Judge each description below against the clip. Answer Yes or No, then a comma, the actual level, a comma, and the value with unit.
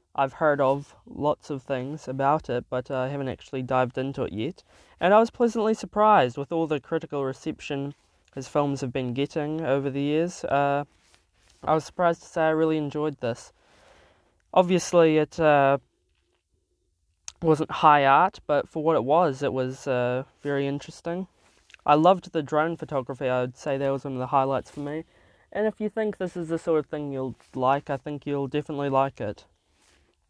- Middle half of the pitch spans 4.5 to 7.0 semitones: No, average, 3.1 semitones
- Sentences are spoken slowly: No, average, 190 wpm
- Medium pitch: Yes, medium, 145 Hz